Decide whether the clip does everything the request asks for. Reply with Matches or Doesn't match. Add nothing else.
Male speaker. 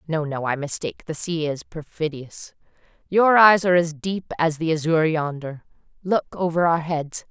Doesn't match